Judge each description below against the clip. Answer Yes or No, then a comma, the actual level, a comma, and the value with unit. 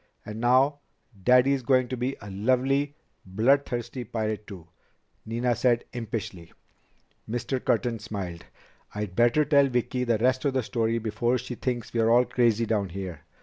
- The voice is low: Yes, low, 120 Hz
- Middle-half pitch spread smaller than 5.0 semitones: Yes, average, 2.9 semitones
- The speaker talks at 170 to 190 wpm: No, average, 155 wpm